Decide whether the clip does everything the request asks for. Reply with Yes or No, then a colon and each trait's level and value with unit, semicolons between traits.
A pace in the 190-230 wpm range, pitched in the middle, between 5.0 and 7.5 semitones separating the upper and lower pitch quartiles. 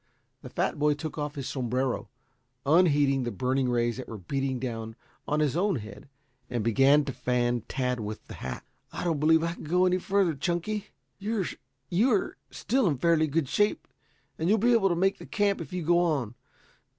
Yes: average, 195 wpm; medium, 145 Hz; wide, 5.6 semitones